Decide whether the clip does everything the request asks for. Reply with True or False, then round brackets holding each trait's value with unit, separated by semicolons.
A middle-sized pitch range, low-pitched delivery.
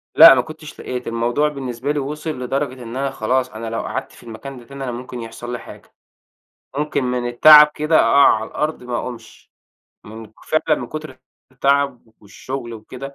True (3.1 semitones; 125 Hz)